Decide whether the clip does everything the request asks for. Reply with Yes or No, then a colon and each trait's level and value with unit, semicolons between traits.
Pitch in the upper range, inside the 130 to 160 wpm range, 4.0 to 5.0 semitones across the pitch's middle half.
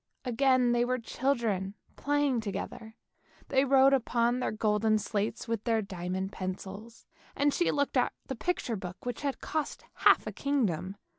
Yes: high, 235 Hz; average, 155 wpm; average, 4.6 semitones